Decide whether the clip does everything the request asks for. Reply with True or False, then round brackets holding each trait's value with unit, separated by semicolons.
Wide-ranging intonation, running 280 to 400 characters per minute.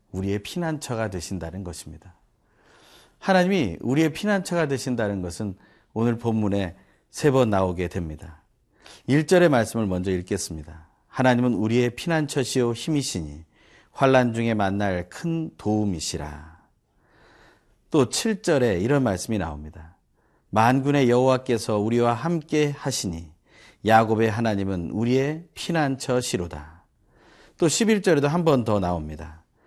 True (6.9 semitones; 285 characters per minute)